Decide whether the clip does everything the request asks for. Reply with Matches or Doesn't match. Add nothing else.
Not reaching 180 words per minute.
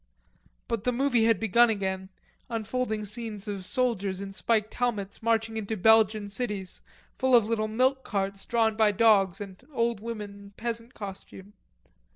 Matches